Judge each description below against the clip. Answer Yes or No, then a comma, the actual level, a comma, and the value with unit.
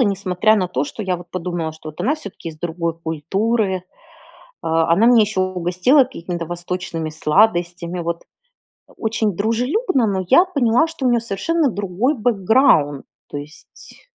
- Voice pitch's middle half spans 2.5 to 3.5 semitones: No, average, 5.3 semitones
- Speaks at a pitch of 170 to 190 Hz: Yes, medium, 185 Hz